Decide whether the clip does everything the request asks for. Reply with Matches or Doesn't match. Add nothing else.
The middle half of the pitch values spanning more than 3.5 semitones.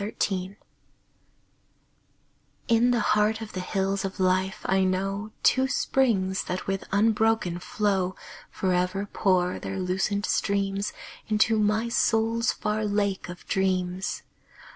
Doesn't match